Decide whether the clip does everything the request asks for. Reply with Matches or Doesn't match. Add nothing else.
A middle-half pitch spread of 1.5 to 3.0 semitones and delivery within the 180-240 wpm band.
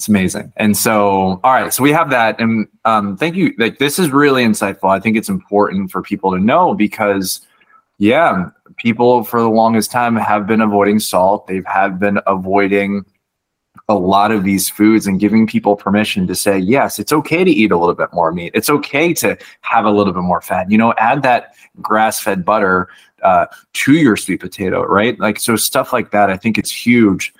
Matches